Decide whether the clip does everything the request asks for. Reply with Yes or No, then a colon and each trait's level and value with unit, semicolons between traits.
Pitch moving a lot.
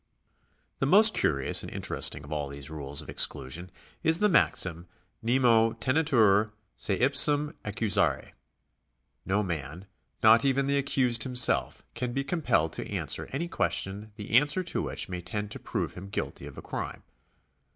Yes: wide, 7.5 semitones